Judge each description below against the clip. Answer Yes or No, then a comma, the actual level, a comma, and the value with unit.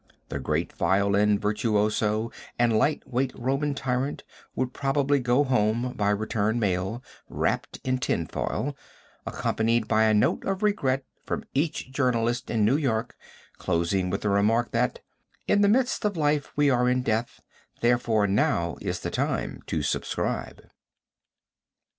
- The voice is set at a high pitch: No, low, 120 Hz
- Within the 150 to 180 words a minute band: No, average, 140 wpm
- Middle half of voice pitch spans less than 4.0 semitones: No, average, 4.3 semitones